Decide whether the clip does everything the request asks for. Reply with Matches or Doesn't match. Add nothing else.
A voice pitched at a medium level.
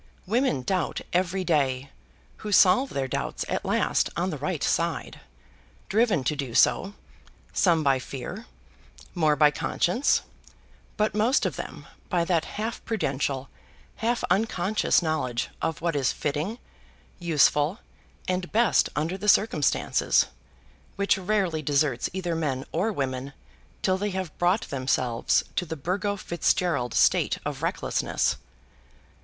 Matches